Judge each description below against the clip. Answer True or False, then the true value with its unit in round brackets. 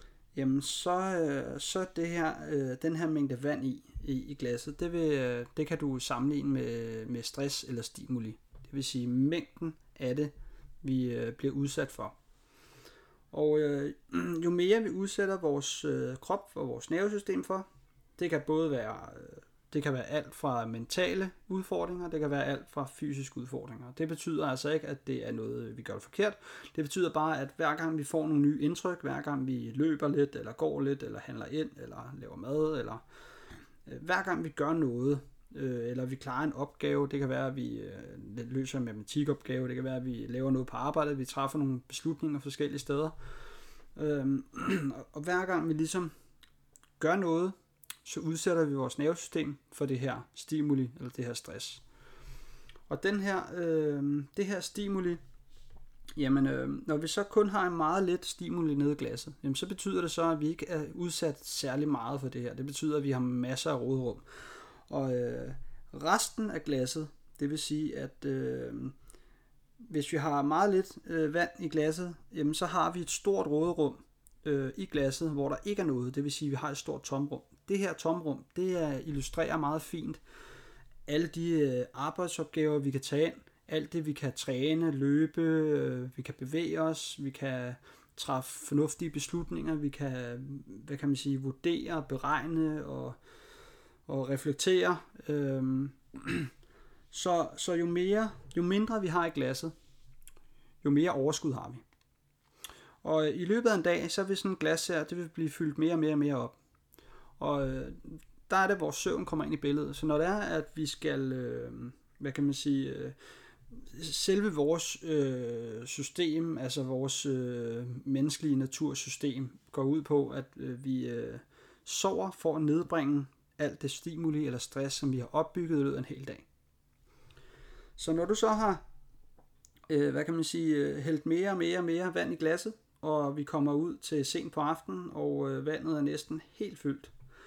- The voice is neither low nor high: True (150 Hz)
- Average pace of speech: True (175 wpm)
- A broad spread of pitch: False (3.3 semitones)